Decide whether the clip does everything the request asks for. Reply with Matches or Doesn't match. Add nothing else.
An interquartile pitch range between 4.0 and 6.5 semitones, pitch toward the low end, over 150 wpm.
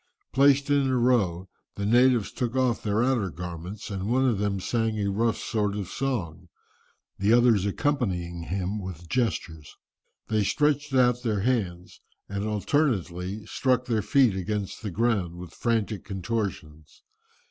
Doesn't match